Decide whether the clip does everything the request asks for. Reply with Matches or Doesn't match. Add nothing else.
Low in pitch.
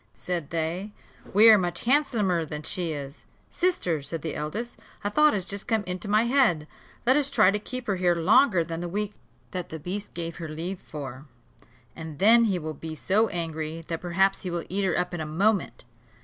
Doesn't match